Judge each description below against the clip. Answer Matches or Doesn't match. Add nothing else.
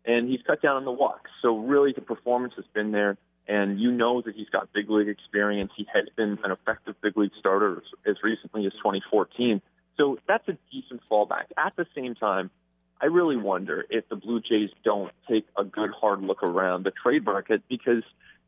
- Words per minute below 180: Doesn't match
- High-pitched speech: Doesn't match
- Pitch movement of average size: Matches